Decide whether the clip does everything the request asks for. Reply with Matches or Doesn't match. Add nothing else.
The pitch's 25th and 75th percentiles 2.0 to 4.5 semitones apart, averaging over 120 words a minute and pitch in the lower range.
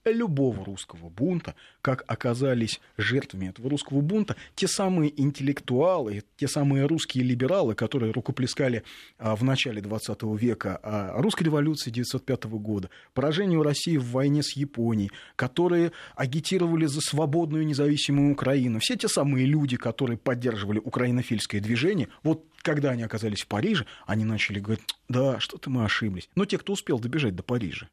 Doesn't match